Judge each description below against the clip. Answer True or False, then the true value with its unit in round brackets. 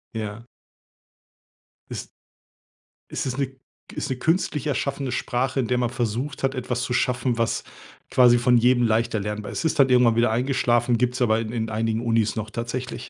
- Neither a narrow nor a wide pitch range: False (2.1 semitones)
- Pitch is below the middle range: True (120 Hz)